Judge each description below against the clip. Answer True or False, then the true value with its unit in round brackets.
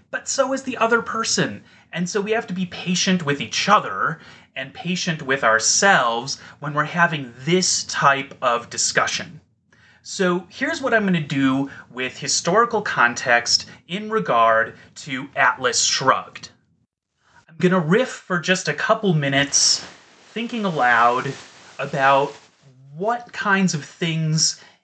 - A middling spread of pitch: False (6.1 semitones)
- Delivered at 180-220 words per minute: False (140 wpm)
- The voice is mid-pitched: True (165 Hz)